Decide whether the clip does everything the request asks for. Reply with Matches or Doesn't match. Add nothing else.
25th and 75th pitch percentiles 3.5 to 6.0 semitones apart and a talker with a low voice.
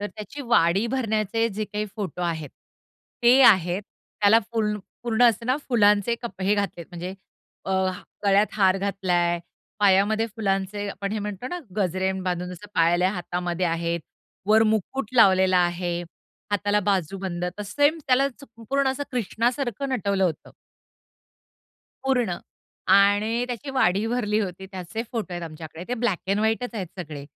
Doesn't match